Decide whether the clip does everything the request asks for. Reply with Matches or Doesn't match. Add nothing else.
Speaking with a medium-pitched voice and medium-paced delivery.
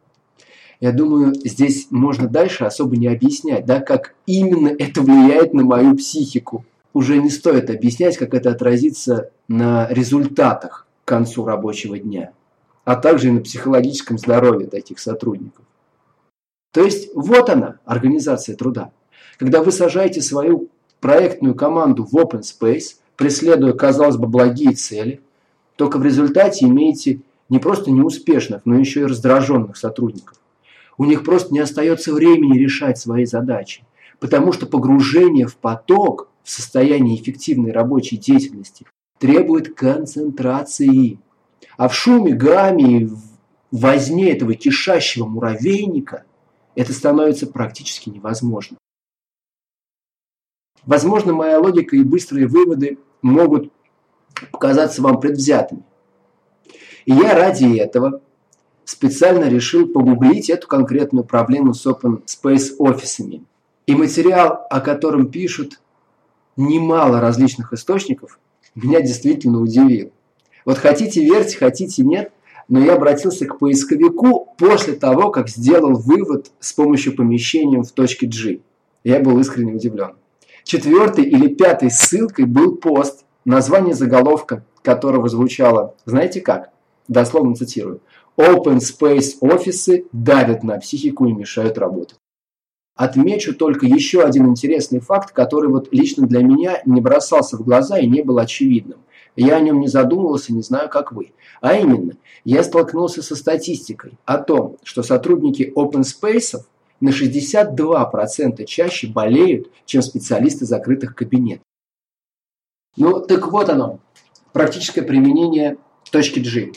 Matches